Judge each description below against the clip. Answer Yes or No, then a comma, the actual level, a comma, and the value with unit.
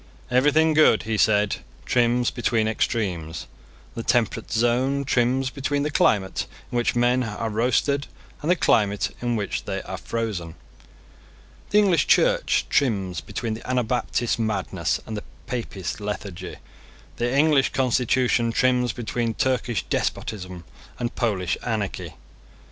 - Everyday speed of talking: No, slow, 130 wpm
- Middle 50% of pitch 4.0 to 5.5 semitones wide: No, average, 3.4 semitones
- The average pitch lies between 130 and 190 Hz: No, low, 120 Hz